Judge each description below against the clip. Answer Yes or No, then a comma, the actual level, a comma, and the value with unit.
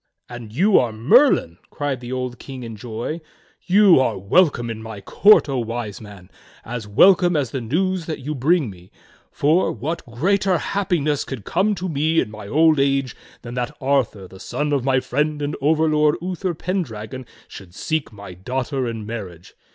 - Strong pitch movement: Yes, wide, 6.0 semitones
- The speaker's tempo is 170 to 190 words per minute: Yes, average, 180 wpm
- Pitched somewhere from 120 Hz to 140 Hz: Yes, low, 135 Hz